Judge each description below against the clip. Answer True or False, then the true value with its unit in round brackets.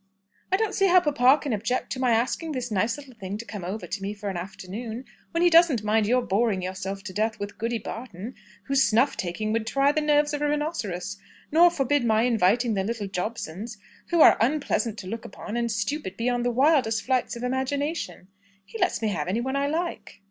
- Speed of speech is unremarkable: False (215 wpm)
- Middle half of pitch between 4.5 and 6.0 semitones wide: True (5.1 semitones)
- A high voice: True (230 Hz)